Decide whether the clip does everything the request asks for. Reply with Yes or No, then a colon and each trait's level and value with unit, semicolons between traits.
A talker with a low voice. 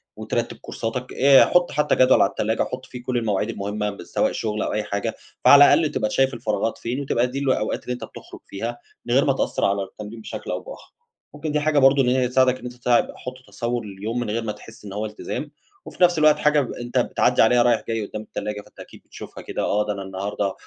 Yes: low, 120 Hz